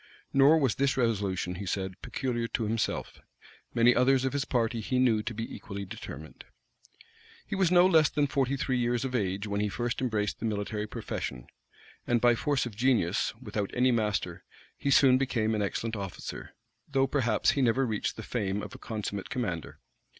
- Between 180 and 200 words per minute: Yes, average, 185 wpm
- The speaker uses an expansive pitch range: No, average, 4.0 semitones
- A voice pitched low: Yes, low, 115 Hz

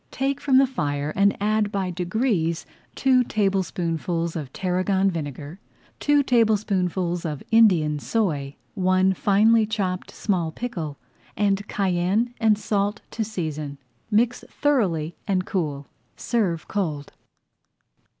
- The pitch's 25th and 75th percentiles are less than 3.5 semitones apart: No, average, 4.7 semitones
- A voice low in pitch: No, high, 190 Hz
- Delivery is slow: Yes, slow, 115 wpm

